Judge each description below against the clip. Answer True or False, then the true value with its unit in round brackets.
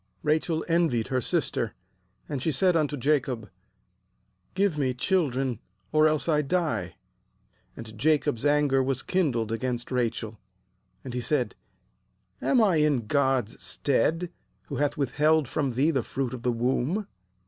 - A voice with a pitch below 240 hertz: True (140 Hz)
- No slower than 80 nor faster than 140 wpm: False (150 wpm)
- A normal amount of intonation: True (4.0 semitones)